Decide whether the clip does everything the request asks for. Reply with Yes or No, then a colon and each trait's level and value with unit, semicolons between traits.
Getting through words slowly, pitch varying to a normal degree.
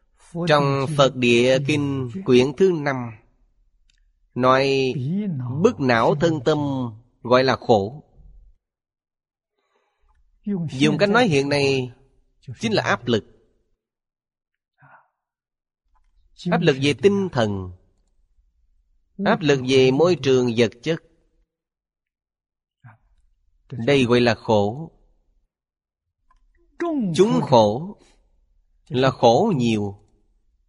No: slow, 90 wpm; wide, 6.9 semitones